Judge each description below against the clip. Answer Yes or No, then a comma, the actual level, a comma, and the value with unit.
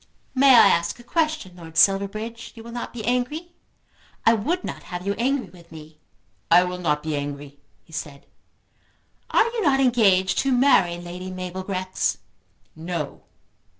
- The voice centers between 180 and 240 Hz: Yes, high, 190 Hz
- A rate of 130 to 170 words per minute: Yes, average, 160 wpm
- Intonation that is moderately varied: No, wide, 6.3 semitones